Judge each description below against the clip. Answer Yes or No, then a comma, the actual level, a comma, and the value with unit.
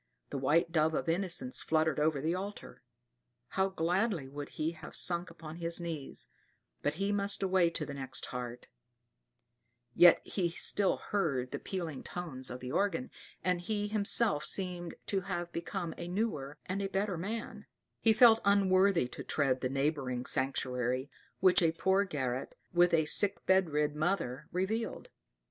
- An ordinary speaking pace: Yes, average, 160 wpm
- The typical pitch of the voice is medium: Yes, medium, 170 Hz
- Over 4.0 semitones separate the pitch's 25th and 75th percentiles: Yes, average, 4.8 semitones